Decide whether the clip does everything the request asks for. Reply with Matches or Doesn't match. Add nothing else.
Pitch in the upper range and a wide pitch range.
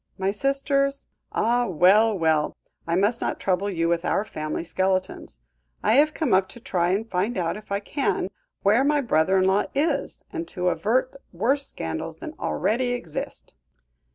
Matches